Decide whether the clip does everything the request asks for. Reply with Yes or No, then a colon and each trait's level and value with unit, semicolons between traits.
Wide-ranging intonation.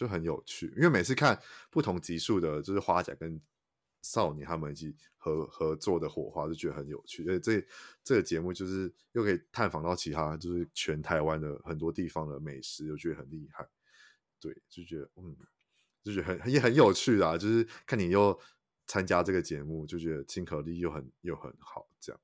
No: average, 3.0 semitones